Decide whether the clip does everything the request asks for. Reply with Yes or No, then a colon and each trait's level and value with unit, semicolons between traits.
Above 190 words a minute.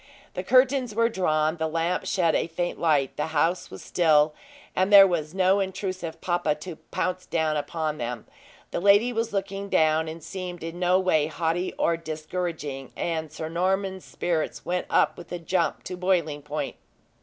No: average, 175 wpm